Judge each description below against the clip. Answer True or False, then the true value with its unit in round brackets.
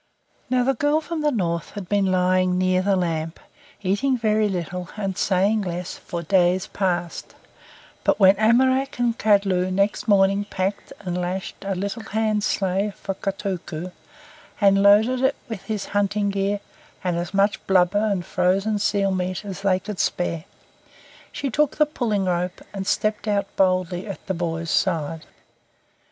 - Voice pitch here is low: False (195 Hz)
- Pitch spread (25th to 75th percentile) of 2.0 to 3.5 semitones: True (2.6 semitones)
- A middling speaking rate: True (160 wpm)